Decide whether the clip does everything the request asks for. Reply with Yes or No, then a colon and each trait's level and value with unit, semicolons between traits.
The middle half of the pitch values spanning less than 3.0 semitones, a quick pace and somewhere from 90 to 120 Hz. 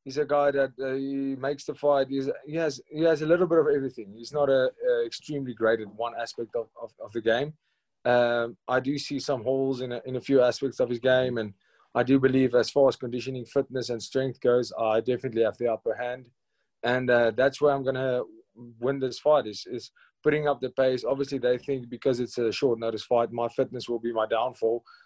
No: narrow, 2.6 semitones; fast, 230 wpm; low, 130 Hz